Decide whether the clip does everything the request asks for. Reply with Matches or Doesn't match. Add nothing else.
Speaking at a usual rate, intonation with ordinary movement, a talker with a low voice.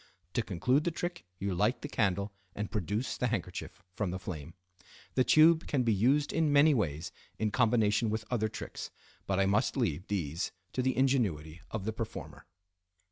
Matches